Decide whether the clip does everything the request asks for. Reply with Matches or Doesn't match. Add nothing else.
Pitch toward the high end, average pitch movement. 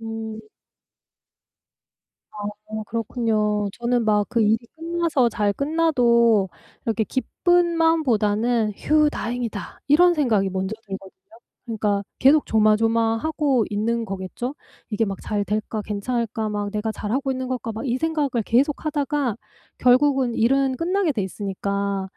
Matches